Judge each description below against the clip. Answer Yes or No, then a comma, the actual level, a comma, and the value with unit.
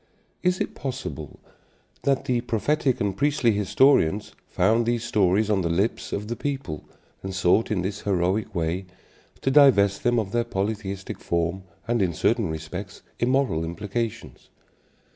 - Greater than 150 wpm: No, average, 145 wpm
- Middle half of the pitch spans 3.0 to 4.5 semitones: Yes, average, 4.2 semitones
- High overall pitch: No, low, 105 Hz